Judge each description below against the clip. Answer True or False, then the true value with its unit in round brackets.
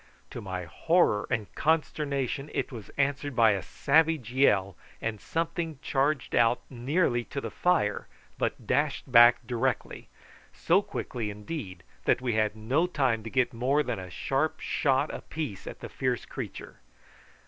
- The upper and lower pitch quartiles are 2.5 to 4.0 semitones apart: False (4.7 semitones)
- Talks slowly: False (150 wpm)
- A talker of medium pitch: False (130 Hz)